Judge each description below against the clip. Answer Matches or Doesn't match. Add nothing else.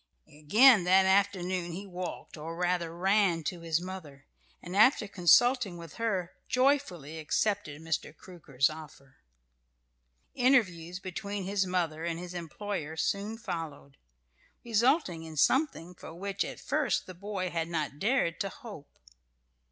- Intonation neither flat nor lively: Matches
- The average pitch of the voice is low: Doesn't match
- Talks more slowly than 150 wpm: Matches